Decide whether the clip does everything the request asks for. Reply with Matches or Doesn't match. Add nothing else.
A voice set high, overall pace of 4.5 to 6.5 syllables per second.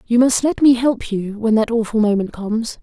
Matches